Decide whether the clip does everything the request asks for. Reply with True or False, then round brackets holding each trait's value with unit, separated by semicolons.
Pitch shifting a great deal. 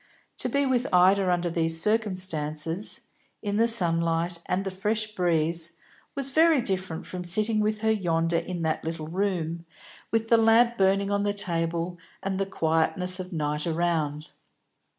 False (4.1 semitones)